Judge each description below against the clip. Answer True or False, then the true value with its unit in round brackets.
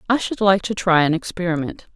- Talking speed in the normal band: False (215 wpm)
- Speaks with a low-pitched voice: False (185 Hz)